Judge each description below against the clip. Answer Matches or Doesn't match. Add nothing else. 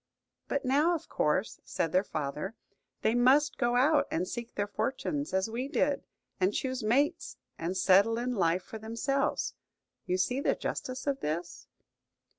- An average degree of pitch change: Doesn't match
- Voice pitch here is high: Matches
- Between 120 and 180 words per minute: Matches